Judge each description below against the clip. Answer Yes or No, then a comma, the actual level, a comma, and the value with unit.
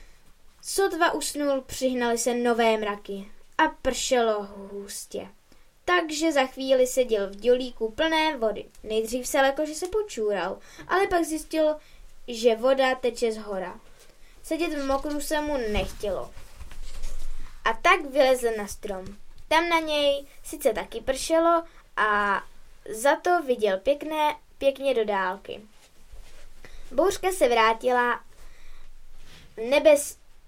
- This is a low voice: No, very high, 265 Hz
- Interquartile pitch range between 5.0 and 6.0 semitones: Yes, wide, 5.6 semitones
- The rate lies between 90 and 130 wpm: Yes, average, 120 wpm